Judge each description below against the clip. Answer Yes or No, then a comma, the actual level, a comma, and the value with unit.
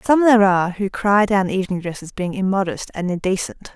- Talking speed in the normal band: No, fast, 210 wpm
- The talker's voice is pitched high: Yes, high, 195 Hz